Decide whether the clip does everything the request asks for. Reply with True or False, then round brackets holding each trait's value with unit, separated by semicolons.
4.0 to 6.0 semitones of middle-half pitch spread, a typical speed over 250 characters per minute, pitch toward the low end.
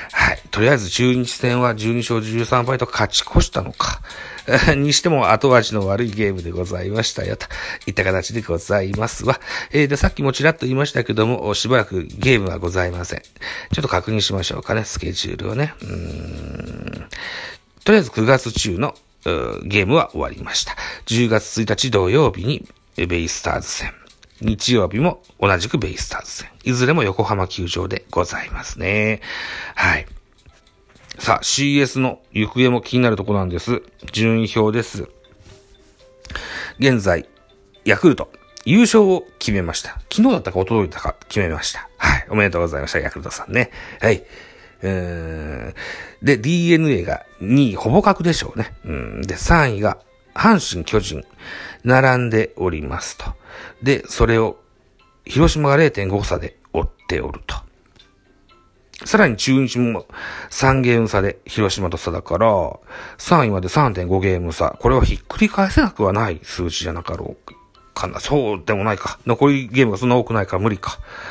True (5.6 semitones; 310 characters per minute; 110 Hz)